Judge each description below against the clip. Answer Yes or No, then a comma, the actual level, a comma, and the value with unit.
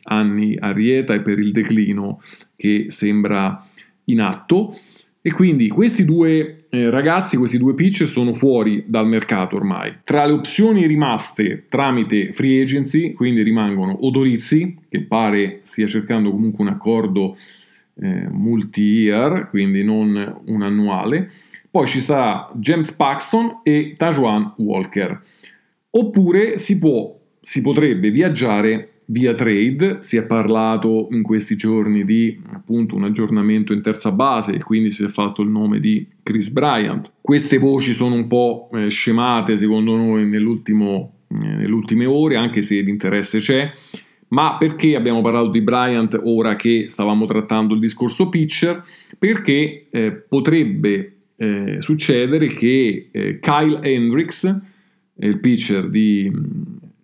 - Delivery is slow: No, average, 135 wpm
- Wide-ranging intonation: Yes, wide, 6.7 semitones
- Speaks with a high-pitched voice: No, low, 120 Hz